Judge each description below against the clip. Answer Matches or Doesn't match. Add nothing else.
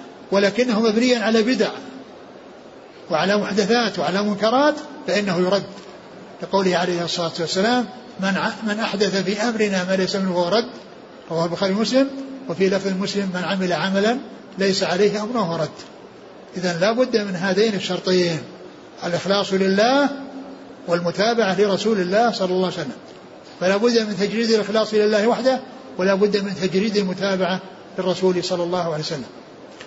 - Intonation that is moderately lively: Matches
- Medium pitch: Doesn't match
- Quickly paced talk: Matches